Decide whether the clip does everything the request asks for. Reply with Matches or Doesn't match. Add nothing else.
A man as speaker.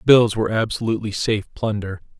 Matches